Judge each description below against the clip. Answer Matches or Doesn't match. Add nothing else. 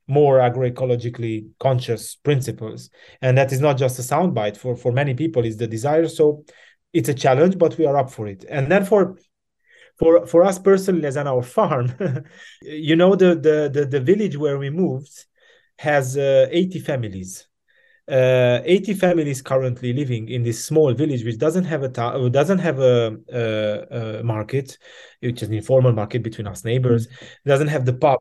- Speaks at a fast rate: Doesn't match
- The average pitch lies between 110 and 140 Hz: Matches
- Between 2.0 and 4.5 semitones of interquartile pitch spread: Doesn't match